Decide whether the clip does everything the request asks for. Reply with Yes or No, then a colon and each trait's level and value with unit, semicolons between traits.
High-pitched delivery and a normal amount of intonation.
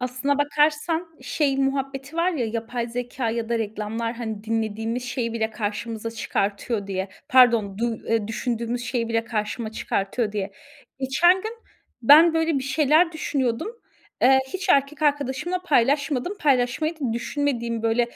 Yes: high, 245 Hz; average, 4.2 semitones